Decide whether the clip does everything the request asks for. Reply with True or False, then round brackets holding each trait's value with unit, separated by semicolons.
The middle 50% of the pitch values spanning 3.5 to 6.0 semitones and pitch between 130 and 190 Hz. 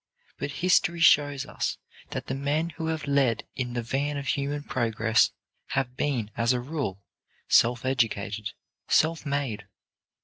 True (3.8 semitones; 135 Hz)